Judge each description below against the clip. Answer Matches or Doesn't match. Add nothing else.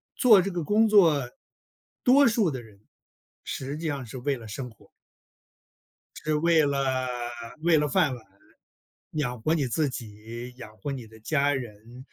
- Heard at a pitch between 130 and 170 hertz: Matches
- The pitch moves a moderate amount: Matches